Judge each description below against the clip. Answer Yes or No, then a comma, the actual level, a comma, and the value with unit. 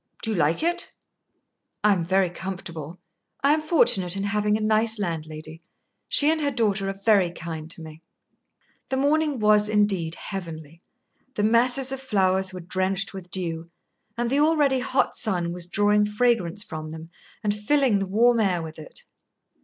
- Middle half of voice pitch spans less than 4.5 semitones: No, average, 5.3 semitones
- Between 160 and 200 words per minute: Yes, average, 170 wpm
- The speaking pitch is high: Yes, high, 195 Hz